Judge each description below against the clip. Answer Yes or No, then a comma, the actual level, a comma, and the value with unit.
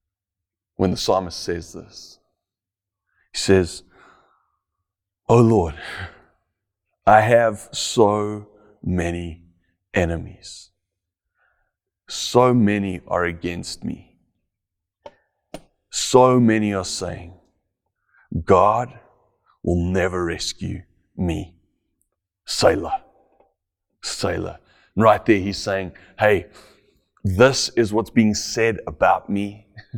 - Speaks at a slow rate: Yes, slow, 85 wpm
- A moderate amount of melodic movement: Yes, average, 3.1 semitones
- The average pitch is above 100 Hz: No, very low, 95 Hz